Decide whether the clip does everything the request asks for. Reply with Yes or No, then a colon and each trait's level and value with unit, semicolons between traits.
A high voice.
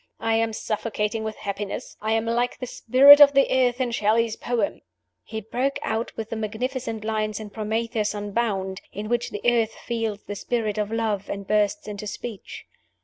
Yes: high, 220 Hz